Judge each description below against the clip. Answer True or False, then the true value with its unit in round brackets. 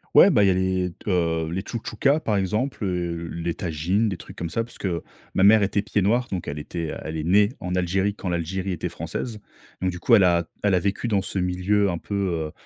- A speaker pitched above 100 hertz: False (95 Hz)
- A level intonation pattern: False (3.1 semitones)